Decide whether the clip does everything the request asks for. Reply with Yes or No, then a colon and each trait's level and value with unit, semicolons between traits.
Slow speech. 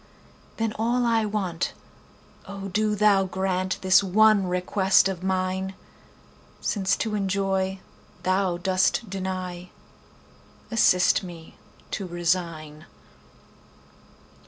Yes: slow, 80 wpm